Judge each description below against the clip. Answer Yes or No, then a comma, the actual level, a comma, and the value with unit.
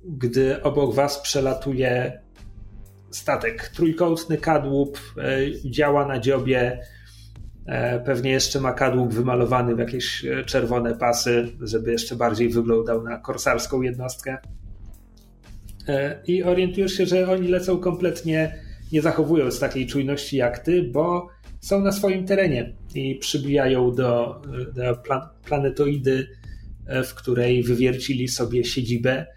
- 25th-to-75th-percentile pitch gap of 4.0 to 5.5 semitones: No, average, 3.3 semitones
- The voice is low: Yes, low, 130 Hz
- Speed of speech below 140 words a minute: Yes, slow, 110 wpm